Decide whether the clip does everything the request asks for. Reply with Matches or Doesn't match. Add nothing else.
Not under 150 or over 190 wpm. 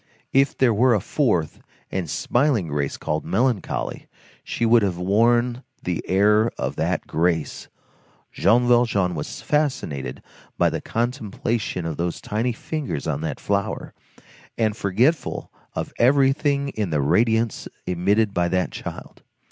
Doesn't match